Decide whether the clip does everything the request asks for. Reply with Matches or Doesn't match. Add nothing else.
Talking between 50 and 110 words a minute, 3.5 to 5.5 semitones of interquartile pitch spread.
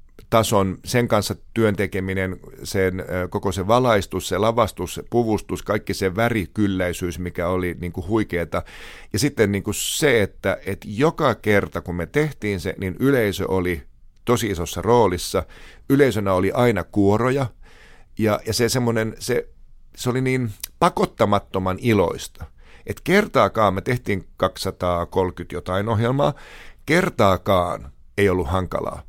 Doesn't match